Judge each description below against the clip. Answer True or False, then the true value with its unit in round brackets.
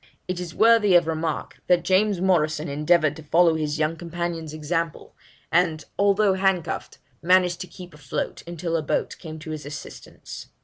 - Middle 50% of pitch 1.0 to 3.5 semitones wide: True (2.7 semitones)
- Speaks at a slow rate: False (165 wpm)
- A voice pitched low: False (170 Hz)